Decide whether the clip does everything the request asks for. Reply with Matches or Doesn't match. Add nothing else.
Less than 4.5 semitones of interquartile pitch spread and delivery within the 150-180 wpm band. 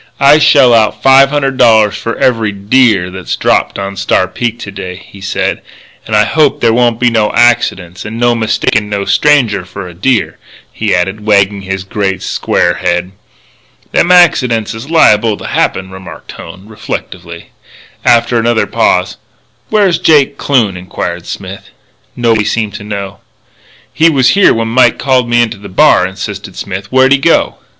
Matches